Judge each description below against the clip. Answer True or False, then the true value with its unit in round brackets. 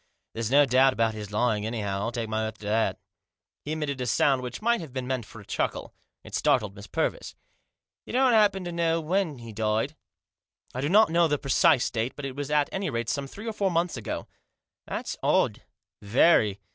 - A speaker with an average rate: False (220 wpm)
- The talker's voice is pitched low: True (130 Hz)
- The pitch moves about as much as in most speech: False (6.8 semitones)